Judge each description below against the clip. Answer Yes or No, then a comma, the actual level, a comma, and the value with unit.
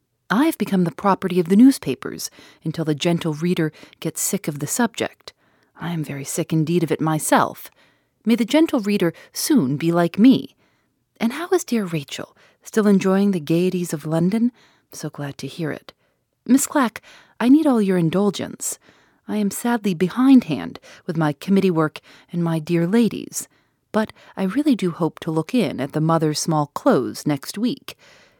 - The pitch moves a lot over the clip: Yes, wide, 6.3 semitones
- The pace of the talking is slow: No, average, 175 wpm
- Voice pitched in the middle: Yes, medium, 180 Hz